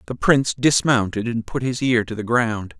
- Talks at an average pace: No, fast, 215 wpm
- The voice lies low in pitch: Yes, low, 120 Hz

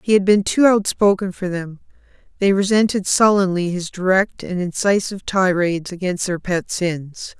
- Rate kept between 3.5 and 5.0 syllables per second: Yes, 4.8 syllables/s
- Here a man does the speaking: No, female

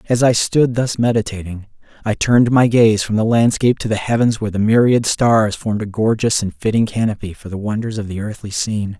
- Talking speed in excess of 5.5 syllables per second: Yes, 5.8 syllables/s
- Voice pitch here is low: Yes, low, 110 Hz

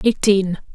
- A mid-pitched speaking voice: No, high, 195 Hz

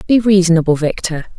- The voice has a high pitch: No, medium, 180 Hz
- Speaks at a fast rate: No, slow, 130 wpm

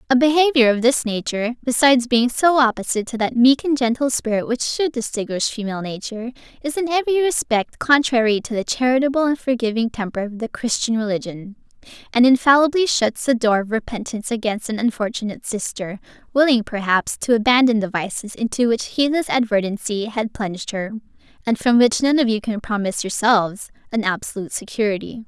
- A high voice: Yes, high, 235 Hz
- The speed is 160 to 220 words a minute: Yes, average, 170 wpm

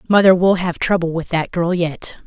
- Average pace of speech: No, fast, 210 wpm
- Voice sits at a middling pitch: Yes, medium, 175 Hz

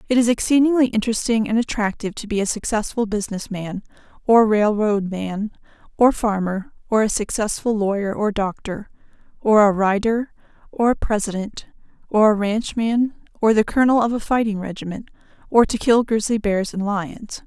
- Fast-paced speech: No, average, 160 wpm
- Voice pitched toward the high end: Yes, high, 215 Hz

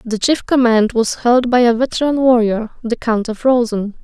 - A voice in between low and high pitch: No, high, 235 Hz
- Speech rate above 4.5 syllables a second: Yes, 4.8 syllables/s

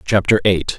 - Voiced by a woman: No, male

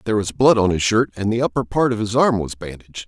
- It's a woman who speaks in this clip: No, male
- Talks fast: Yes, fast, 295 wpm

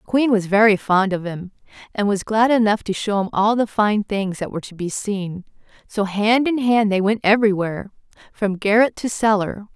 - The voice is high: Yes, high, 205 Hz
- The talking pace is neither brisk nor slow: No, fast, 210 wpm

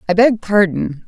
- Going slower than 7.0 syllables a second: Yes, 4.5 syllables/s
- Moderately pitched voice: No, high, 200 Hz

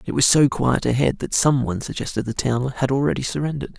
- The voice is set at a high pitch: No, low, 135 Hz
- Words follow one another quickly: Yes, fast, 220 wpm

